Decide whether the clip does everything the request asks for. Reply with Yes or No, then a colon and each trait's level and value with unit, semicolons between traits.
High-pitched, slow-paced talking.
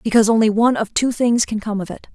No: high, 220 Hz; fast, 280 wpm